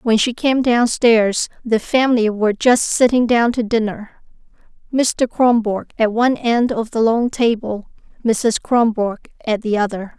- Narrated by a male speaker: No, female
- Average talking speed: Yes, average, 155 wpm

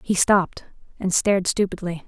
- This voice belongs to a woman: Yes, female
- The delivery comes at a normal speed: Yes, average, 145 wpm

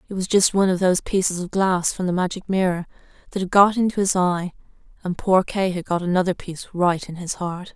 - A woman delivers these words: Yes, female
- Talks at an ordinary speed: No, fast, 230 wpm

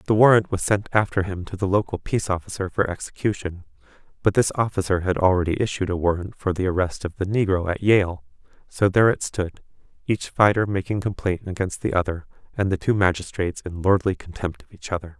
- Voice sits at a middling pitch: No, very low, 95 Hz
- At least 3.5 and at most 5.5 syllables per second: No, 5.9 syllables/s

